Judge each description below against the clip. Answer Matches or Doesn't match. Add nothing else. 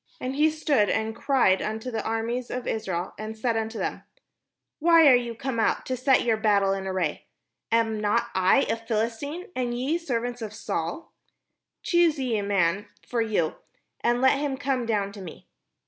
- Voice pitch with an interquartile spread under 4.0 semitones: Matches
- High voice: Matches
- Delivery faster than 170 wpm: Matches